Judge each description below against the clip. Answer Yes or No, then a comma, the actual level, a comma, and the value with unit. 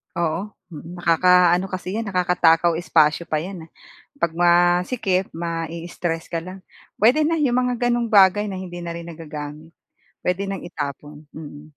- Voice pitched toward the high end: No, medium, 175 Hz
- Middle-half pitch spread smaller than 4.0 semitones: Yes, average, 2.8 semitones